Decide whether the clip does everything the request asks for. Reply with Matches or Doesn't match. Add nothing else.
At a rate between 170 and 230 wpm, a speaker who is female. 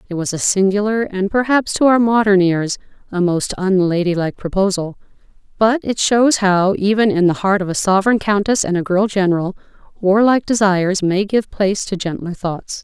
Matches